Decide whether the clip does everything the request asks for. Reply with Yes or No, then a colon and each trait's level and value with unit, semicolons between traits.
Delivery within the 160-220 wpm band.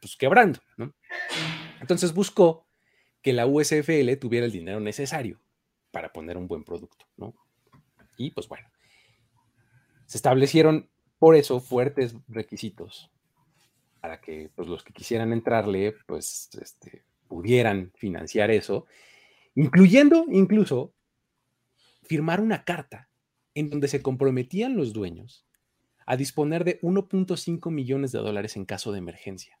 No: slow, 125 wpm